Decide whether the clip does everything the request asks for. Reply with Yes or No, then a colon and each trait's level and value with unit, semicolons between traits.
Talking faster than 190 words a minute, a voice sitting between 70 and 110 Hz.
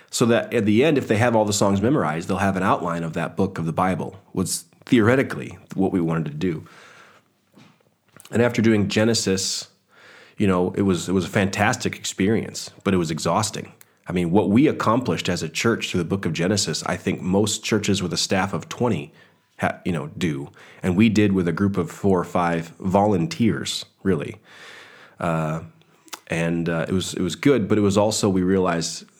Yes: average, 200 wpm; very low, 95 Hz